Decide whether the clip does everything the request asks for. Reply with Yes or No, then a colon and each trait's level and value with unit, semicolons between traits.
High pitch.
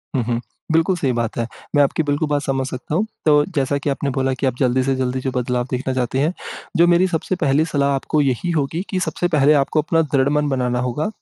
No: medium, 140 Hz